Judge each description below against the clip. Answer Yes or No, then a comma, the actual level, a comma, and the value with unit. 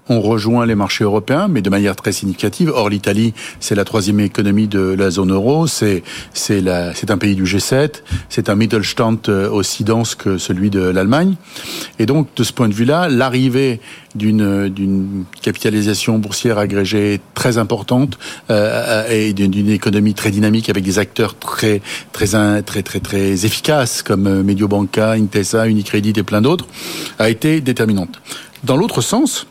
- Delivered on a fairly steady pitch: Yes, narrow, 2.3 semitones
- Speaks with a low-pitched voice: Yes, low, 105 Hz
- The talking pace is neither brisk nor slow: Yes, average, 165 wpm